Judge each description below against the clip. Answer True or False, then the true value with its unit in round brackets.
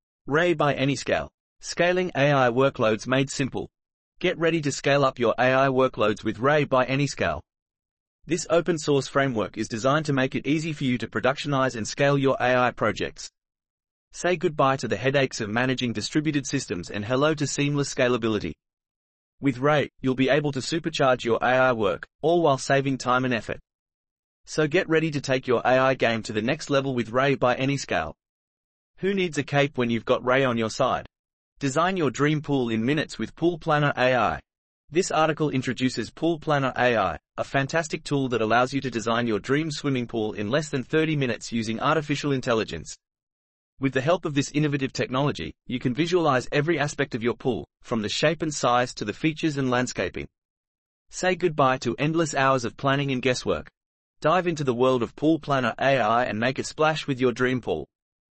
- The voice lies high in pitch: False (135 Hz)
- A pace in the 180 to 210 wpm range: True (185 wpm)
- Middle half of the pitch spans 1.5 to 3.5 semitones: True (3.1 semitones)